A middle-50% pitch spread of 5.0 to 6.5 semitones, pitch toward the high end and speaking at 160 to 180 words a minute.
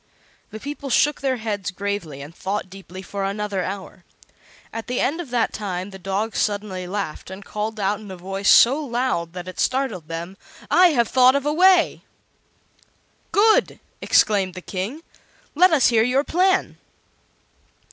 Yes: wide, 5.6 semitones; high, 210 Hz; average, 165 wpm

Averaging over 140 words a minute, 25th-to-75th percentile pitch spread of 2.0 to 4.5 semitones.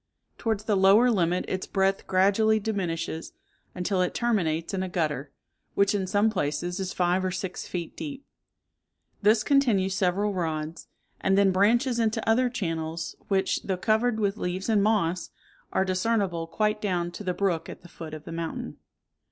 Yes: average, 170 wpm; average, 3.3 semitones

